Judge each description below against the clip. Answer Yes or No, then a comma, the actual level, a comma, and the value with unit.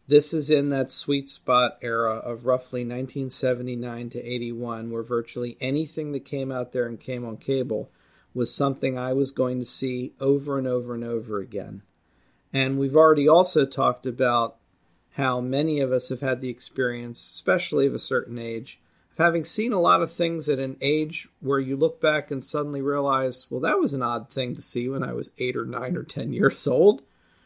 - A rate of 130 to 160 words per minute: No, average, 195 wpm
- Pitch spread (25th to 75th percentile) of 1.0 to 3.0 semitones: Yes, narrow, 2.6 semitones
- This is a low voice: Yes, low, 130 Hz